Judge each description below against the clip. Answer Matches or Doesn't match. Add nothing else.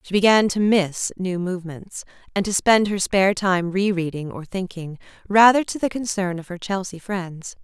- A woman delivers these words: Matches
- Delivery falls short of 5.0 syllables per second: Matches